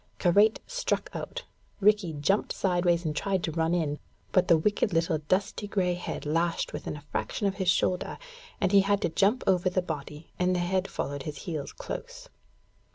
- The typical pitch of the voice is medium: Yes, medium, 180 Hz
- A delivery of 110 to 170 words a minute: No, average, 185 wpm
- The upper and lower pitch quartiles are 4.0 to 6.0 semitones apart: No, average, 3.4 semitones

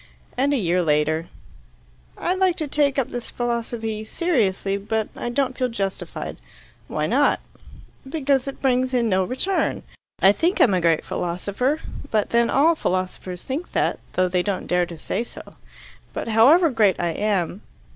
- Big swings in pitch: Yes, wide, 6.4 semitones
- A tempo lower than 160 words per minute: No, average, 165 wpm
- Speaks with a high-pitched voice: Yes, high, 225 Hz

